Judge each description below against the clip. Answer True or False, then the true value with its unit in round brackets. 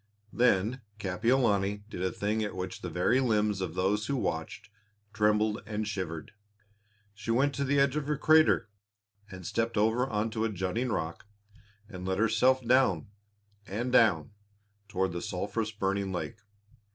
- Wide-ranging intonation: False (3.9 semitones)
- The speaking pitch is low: True (105 Hz)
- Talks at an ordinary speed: True (150 wpm)